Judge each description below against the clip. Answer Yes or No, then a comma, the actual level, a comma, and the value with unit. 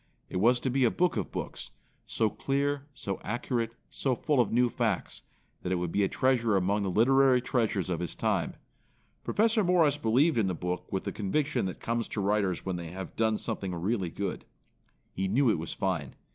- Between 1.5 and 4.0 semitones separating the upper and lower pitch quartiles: No, wide, 5.5 semitones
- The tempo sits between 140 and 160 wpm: No, fast, 205 wpm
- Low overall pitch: Yes, low, 110 Hz